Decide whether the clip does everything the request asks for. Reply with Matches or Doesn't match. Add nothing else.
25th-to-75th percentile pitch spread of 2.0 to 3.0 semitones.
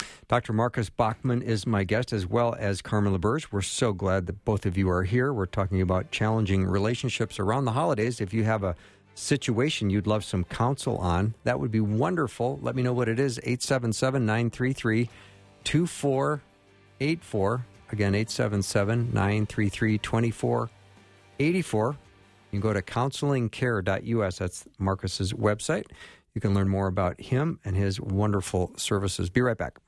Doesn't match